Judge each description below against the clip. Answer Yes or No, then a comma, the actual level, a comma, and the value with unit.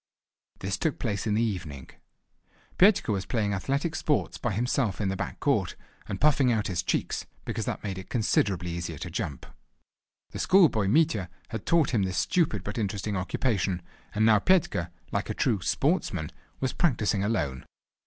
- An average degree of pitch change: No, wide, 5.9 semitones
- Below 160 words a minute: No, average, 170 wpm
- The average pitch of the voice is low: Yes, low, 105 Hz